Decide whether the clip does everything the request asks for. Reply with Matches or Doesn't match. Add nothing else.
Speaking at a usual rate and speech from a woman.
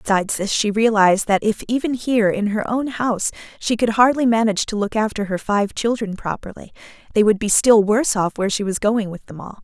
Doesn't match